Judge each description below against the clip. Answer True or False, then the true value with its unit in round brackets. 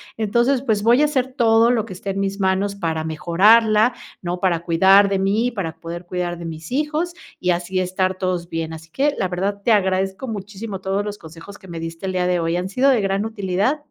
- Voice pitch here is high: True (195 Hz)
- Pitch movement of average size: True (3.8 semitones)